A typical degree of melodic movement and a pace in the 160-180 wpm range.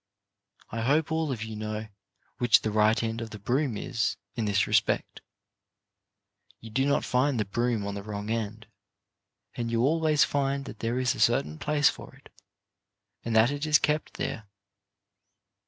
Yes: average, 4.4 semitones; average, 170 wpm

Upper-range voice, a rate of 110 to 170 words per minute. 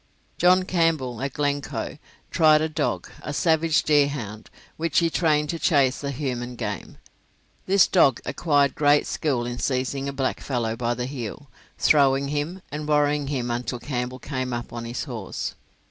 No: medium, 140 Hz; average, 160 wpm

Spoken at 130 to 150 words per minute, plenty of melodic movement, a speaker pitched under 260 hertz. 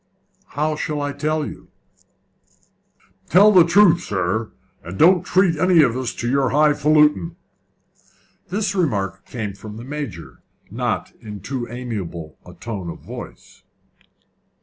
Yes: slow, 135 wpm; wide, 7.4 semitones; medium, 140 Hz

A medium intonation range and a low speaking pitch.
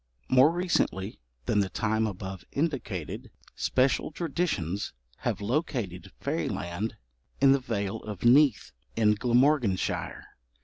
No: wide, 5.9 semitones; low, 110 Hz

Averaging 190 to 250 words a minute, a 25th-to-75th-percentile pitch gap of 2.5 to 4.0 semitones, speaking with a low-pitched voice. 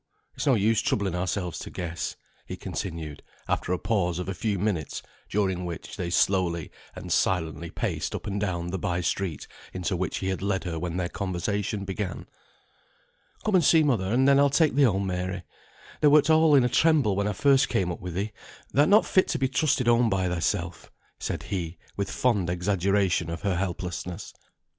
No: average, 195 wpm; average, 4.5 semitones; very low, 95 Hz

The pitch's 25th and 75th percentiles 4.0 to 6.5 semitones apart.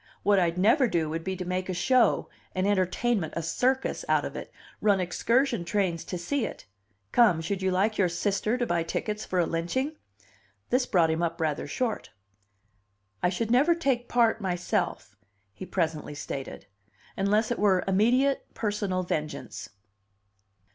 Yes: average, 5.2 semitones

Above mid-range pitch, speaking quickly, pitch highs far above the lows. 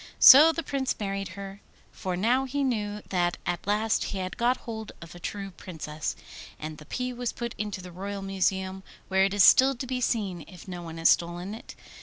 No: high, 195 Hz; fast, 210 wpm; average, 4.6 semitones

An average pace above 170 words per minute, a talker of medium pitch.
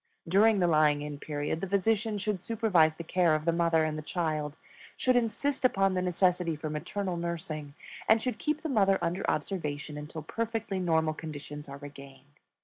Yes: average, 180 wpm; medium, 170 Hz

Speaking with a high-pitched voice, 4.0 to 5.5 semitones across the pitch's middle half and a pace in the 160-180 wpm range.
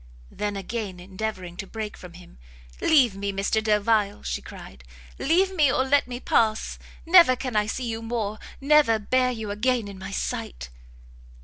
Yes: high, 220 Hz; average, 4.3 semitones; average, 170 wpm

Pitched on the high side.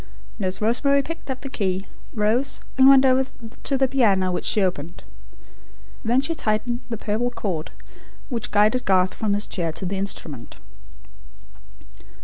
Yes: high, 215 Hz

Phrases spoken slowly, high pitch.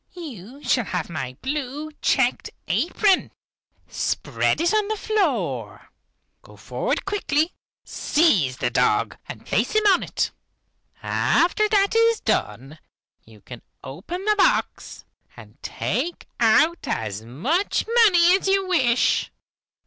Yes: slow, 125 wpm; very high, 315 Hz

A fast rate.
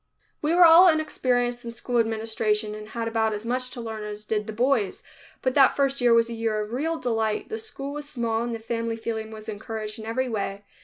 Yes: fast, 225 wpm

